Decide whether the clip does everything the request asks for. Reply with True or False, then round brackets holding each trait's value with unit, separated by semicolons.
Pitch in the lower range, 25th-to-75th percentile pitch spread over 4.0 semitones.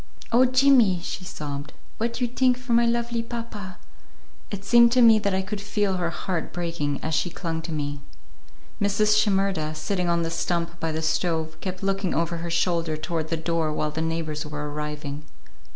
False (175 Hz; 4.7 semitones)